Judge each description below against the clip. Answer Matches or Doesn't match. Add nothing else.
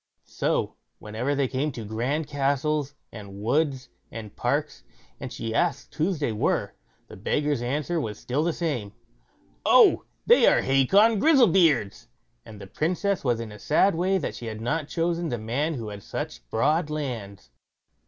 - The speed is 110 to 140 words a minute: Doesn't match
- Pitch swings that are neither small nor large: Doesn't match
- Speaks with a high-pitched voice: Doesn't match